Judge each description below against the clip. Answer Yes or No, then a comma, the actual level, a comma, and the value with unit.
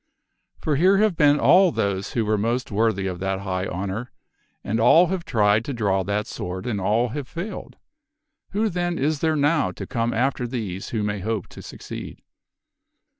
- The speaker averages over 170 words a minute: Yes, average, 180 wpm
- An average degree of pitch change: No, wide, 6.9 semitones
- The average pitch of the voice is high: No, low, 115 Hz